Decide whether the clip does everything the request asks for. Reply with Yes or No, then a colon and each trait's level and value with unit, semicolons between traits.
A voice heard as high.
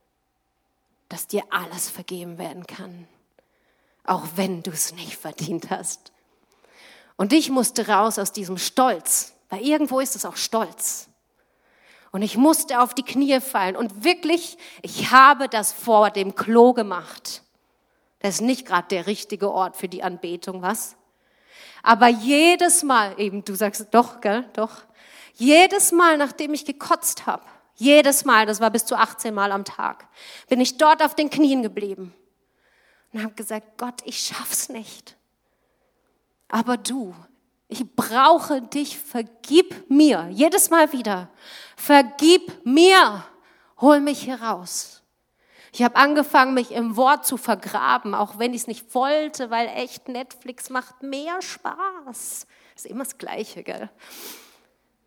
Yes: high, 240 Hz